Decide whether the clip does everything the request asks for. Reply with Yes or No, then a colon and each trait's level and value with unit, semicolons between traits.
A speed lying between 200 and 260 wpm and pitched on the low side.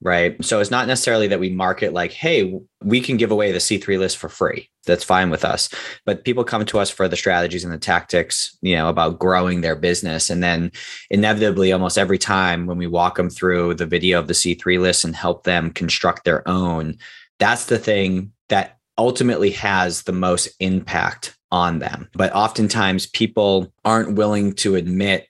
No: average, 190 wpm; very low, 95 Hz